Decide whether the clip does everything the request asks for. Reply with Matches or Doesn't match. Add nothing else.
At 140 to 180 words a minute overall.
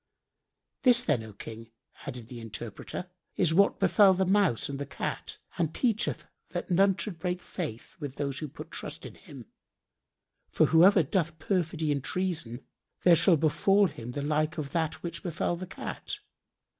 Matches